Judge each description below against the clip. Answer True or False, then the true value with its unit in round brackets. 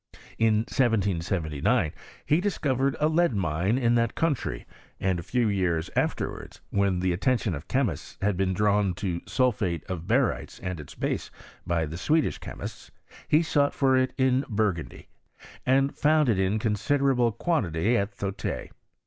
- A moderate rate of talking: True (155 wpm)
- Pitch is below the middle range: True (105 Hz)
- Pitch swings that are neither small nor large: False (6.2 semitones)